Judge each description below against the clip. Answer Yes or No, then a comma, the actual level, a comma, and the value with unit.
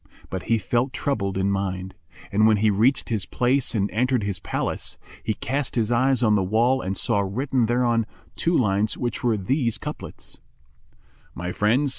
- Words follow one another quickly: No, average, 175 wpm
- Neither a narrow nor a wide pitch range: Yes, average, 4.1 semitones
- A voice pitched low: Yes, low, 110 Hz